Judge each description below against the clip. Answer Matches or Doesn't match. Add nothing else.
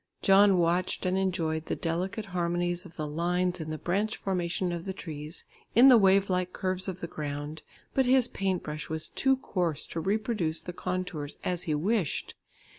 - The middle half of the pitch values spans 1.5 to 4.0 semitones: Matches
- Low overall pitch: Doesn't match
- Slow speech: Doesn't match